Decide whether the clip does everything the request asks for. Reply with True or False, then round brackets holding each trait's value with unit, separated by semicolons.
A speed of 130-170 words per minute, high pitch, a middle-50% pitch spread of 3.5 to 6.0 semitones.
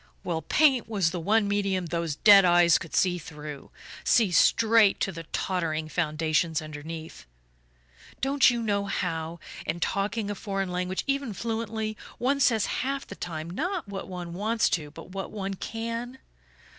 True (155 wpm; 195 Hz; 5.2 semitones)